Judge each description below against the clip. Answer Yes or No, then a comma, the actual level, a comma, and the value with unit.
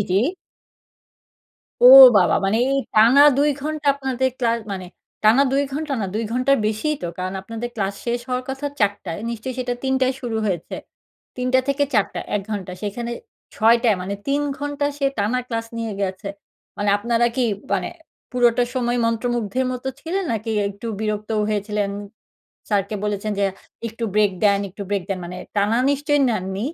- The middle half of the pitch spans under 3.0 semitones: No, average, 4.0 semitones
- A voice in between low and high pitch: No, high, 230 Hz